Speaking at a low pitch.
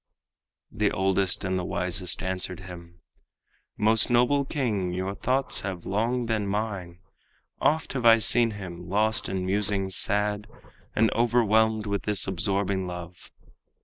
Yes: low, 100 Hz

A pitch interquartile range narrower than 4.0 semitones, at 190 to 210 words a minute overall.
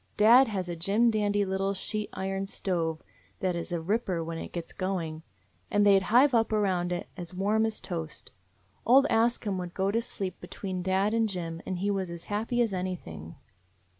Yes: average, 3.3 semitones; average, 195 wpm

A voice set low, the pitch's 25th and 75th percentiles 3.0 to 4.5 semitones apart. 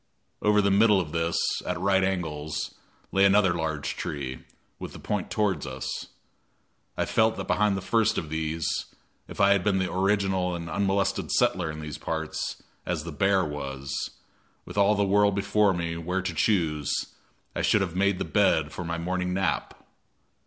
Yes: very low, 90 Hz; average, 3.8 semitones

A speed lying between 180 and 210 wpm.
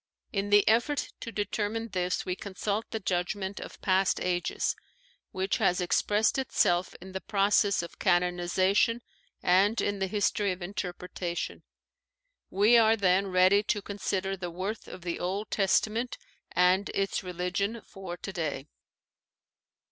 No: average, 140 wpm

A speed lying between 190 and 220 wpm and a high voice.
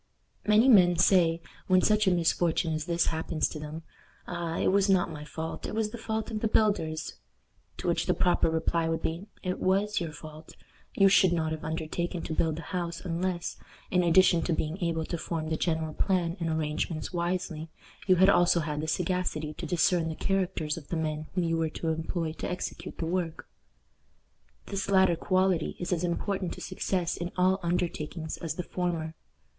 No: average, 195 wpm; medium, 170 Hz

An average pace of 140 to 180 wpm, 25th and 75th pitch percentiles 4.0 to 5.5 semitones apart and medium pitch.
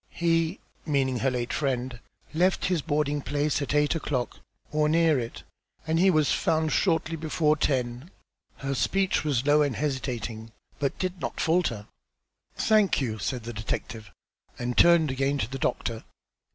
Yes: average, 160 wpm; average, 4.4 semitones; medium, 145 Hz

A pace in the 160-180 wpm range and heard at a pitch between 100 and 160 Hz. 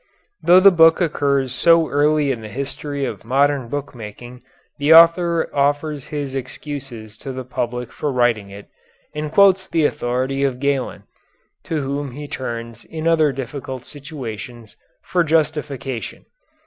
No: average, 145 wpm; medium, 140 Hz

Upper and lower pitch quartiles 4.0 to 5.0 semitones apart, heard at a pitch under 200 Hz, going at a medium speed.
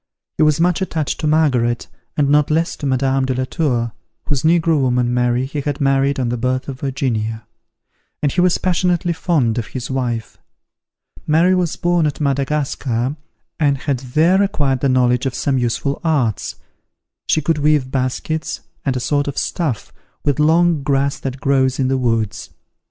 No: average, 3.3 semitones; medium, 140 Hz; average, 175 wpm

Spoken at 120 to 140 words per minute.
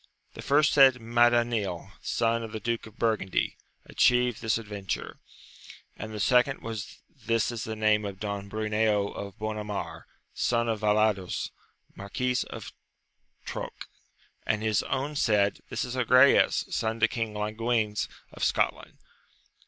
Yes: slow, 135 wpm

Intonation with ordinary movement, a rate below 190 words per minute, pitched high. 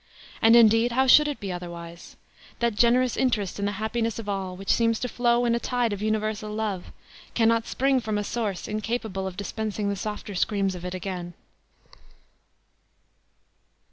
Yes: average, 3.2 semitones; average, 170 wpm; high, 215 Hz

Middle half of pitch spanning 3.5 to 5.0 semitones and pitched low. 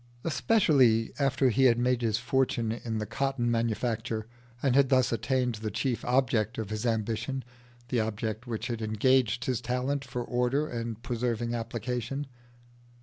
No: narrow, 2.4 semitones; low, 120 Hz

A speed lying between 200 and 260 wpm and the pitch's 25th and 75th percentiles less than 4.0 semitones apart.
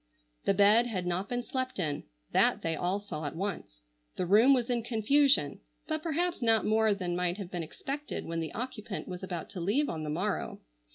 No: fast, 205 wpm; wide, 5.5 semitones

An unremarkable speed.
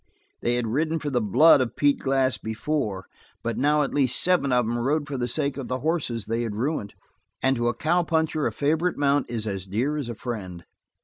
No: fast, 225 wpm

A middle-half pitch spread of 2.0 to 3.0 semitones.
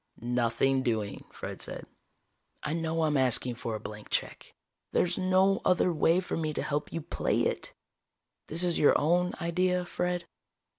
No: wide, 5.5 semitones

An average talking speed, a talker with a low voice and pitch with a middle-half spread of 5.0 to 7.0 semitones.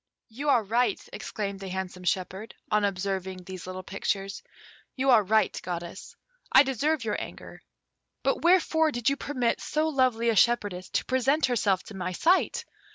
No: average, 160 wpm; high, 215 Hz; wide, 5.5 semitones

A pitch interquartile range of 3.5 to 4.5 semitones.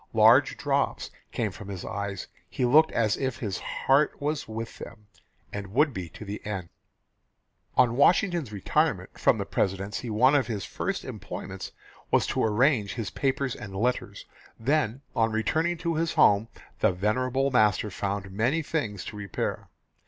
No: average, 5.2 semitones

